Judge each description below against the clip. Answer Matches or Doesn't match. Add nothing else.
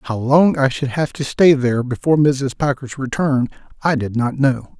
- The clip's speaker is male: Matches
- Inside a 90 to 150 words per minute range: Doesn't match